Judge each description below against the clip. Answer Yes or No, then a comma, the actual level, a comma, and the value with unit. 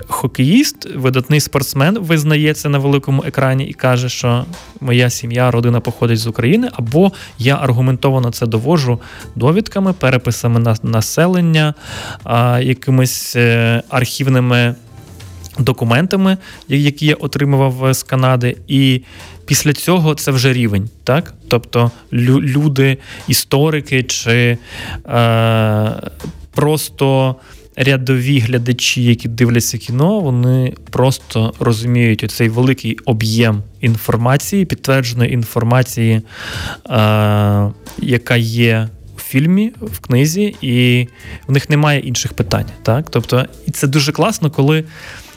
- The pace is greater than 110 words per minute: No, slow, 105 wpm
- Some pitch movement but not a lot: Yes, average, 3.2 semitones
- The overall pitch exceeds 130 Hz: No, low, 125 Hz